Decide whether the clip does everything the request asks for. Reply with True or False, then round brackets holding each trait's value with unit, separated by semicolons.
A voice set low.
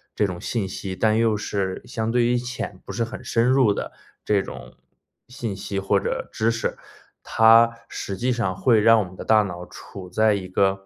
True (105 Hz)